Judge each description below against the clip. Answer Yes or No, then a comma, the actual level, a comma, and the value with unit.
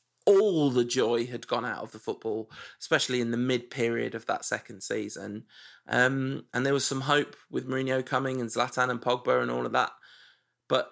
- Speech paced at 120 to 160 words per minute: No, average, 200 wpm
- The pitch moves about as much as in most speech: No, narrow, 1.9 semitones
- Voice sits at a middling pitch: No, low, 125 Hz